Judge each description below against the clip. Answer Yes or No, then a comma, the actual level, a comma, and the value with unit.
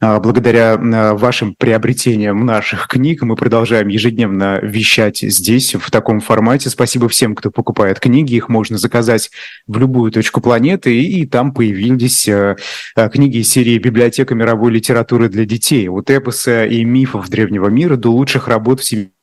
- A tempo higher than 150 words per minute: No, average, 145 wpm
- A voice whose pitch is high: No, low, 115 Hz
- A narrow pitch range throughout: Yes, narrow, 2.3 semitones